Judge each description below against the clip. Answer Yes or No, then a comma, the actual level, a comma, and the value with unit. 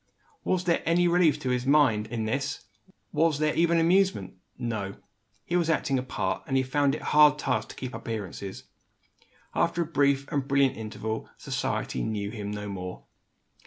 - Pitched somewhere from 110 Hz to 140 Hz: Yes, low, 135 Hz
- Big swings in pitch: Yes, wide, 6.1 semitones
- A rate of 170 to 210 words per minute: Yes, average, 180 wpm